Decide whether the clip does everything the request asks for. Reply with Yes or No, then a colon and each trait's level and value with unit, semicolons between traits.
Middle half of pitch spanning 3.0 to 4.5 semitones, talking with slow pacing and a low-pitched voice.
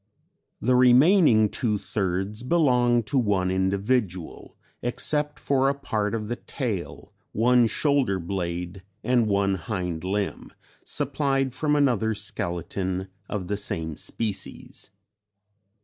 No: average, 5.1 semitones; slow, 115 wpm; low, 105 Hz